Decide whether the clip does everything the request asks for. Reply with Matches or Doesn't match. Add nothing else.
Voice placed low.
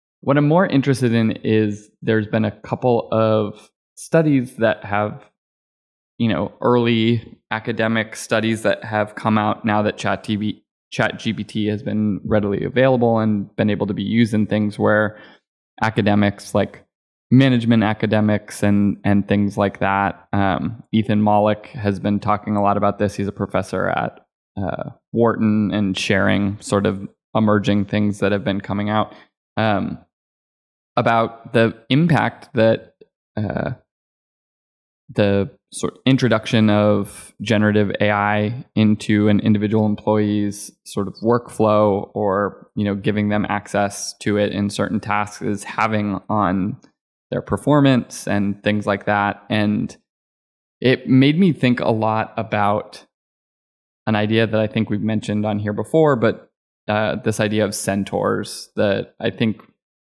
Matches